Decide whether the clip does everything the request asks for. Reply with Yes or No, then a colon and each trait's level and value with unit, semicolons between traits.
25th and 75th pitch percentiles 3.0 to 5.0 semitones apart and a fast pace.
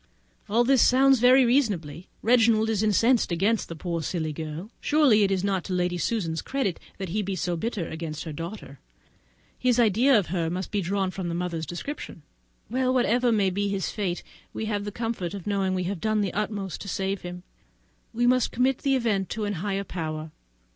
Yes: average, 4.5 semitones; fast, 210 wpm